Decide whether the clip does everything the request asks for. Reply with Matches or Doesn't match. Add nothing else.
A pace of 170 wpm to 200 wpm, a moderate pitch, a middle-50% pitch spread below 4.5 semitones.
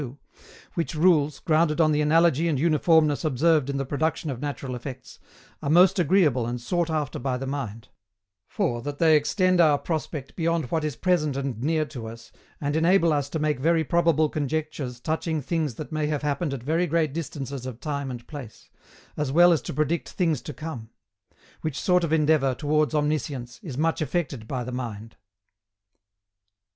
Matches